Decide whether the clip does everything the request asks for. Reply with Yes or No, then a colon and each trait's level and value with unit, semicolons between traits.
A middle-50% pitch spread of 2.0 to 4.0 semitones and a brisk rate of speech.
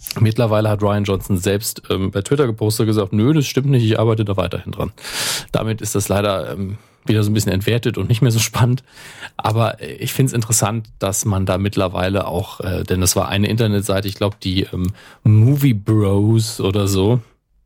Yes: average, 3.2 semitones; fast, 200 wpm